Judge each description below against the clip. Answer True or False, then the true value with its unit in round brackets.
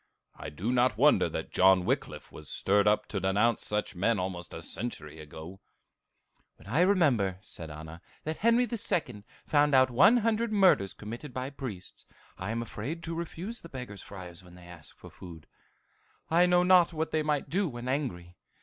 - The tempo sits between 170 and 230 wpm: True (180 wpm)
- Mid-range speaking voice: False (120 Hz)